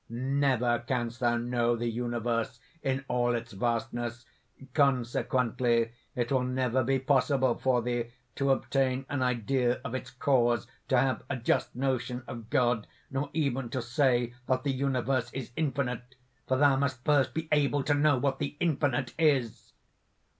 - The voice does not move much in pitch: Yes, narrow, 2.1 semitones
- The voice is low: Yes, low, 130 Hz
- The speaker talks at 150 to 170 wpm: Yes, average, 155 wpm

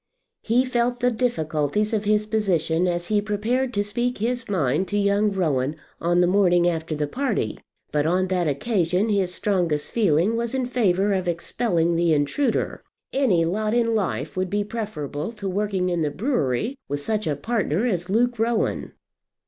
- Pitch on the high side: Yes, high, 200 Hz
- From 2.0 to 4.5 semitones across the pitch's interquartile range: No, average, 5.0 semitones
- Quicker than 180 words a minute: No, average, 175 wpm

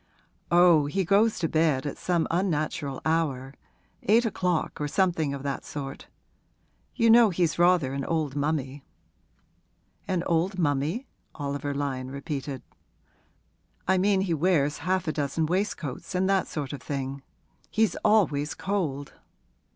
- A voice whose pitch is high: No, medium, 160 Hz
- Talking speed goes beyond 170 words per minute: No, slow, 135 wpm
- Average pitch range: Yes, average, 4.6 semitones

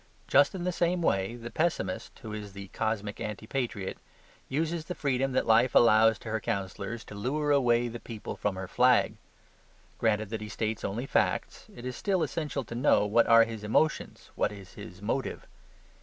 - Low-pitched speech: Yes, low, 115 Hz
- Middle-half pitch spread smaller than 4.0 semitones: No, average, 4.4 semitones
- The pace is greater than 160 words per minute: Yes, average, 185 wpm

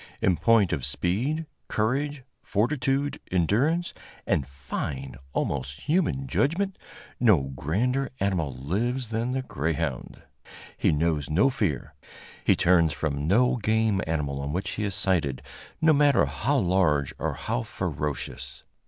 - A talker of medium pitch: No, very low, 95 Hz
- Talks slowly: Yes, slow, 130 wpm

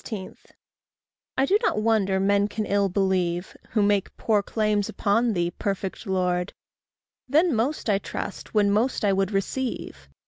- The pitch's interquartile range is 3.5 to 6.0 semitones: No, narrow, 2.5 semitones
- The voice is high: Yes, high, 205 Hz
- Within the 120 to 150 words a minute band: Yes, average, 145 wpm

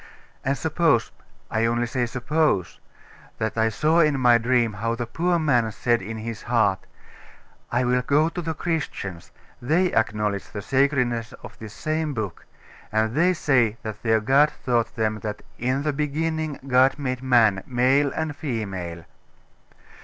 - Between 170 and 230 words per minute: No, average, 155 wpm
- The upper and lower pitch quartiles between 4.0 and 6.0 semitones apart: Yes, average, 4.8 semitones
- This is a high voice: No, low, 125 Hz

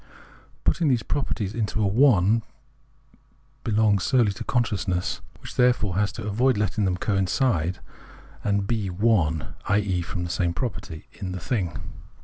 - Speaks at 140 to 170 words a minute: Yes, average, 160 wpm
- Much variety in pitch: No, average, 4.4 semitones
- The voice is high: No, low, 105 Hz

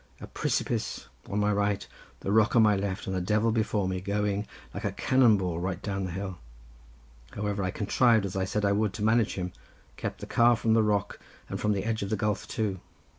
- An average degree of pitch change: No, narrow, 2.1 semitones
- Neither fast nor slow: No, fast, 230 wpm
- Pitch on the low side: Yes, low, 105 Hz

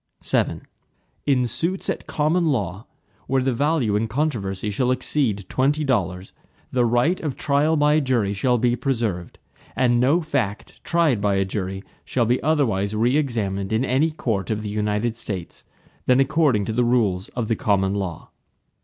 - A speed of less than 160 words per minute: No, average, 165 wpm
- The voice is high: No, low, 120 Hz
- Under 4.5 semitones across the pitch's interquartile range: No, wide, 5.4 semitones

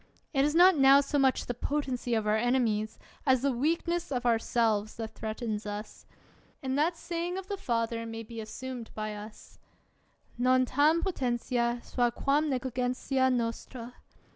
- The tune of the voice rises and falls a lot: No, average, 3.5 semitones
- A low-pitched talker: No, very high, 250 Hz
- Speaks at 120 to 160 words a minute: Yes, average, 155 wpm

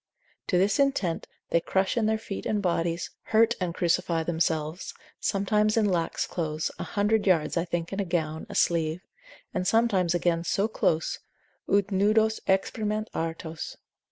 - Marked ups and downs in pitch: No, average, 4.0 semitones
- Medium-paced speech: Yes, average, 155 wpm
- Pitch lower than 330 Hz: Yes, medium, 185 Hz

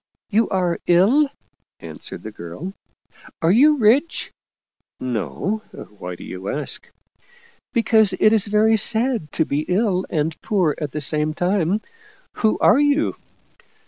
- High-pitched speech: Yes, high, 195 Hz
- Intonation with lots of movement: Yes, wide, 6.4 semitones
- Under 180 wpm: Yes, average, 155 wpm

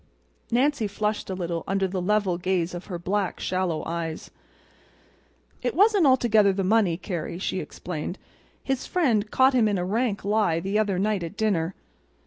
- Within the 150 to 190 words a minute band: Yes, average, 165 wpm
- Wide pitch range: No, average, 3.6 semitones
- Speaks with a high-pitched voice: Yes, high, 195 Hz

